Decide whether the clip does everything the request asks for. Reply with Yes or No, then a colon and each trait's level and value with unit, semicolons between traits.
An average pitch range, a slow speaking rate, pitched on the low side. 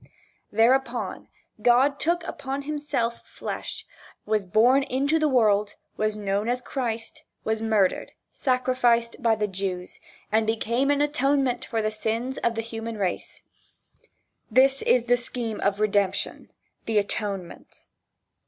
No: average, 3.5 semitones; slow, 130 wpm; high, 230 Hz